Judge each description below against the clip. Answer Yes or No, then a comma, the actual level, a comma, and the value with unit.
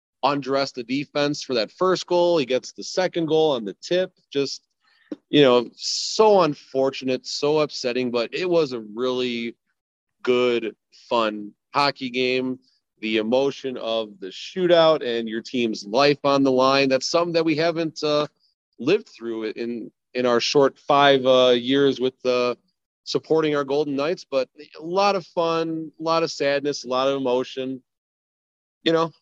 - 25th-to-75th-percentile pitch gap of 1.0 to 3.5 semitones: No, average, 4.1 semitones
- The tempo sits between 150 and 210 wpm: Yes, average, 160 wpm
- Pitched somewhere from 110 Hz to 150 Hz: Yes, low, 135 Hz